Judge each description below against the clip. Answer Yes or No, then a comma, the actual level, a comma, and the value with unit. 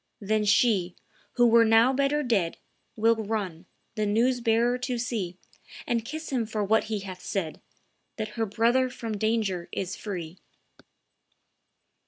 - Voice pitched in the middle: No, high, 220 Hz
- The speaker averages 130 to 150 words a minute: Yes, average, 145 wpm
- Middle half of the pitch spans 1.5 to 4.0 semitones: Yes, average, 3.1 semitones